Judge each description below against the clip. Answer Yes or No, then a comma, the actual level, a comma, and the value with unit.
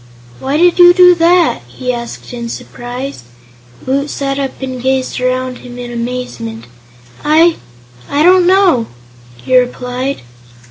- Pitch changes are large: No, average, 4.5 semitones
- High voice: Yes, very high, 260 Hz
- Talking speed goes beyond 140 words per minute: No, slow, 135 wpm